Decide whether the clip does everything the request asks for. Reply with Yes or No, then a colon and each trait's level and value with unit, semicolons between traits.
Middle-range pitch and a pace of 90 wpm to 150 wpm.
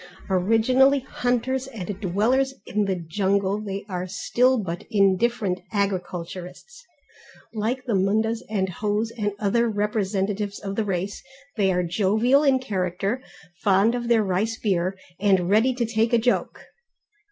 No: high, 210 Hz; average, 140 wpm